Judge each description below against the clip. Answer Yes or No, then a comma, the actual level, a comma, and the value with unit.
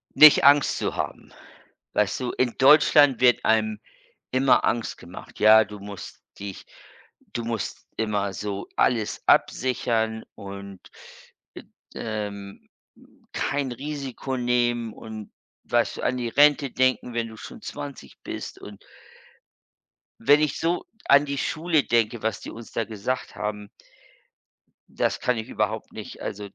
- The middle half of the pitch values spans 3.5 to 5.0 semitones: Yes, average, 3.9 semitones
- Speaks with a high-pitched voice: No, low, 115 Hz